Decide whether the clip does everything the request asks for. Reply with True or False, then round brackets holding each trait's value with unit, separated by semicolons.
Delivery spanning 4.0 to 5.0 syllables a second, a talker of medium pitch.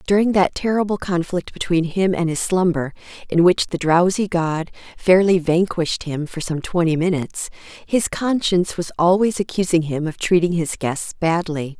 True (4.9 syllables/s; 175 Hz)